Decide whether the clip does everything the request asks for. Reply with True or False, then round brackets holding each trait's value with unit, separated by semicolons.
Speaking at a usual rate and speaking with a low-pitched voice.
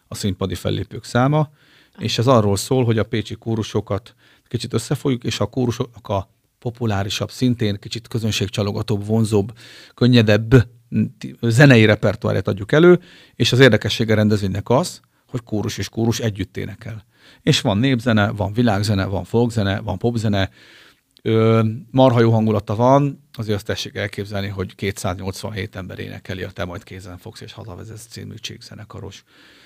True (140 wpm; 110 Hz)